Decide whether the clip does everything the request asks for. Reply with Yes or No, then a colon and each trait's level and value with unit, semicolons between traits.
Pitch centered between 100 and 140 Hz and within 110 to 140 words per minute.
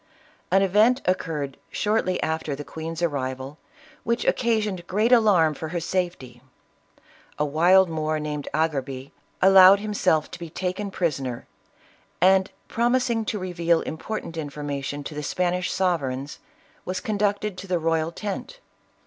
No: medium, 175 Hz; slow, 135 wpm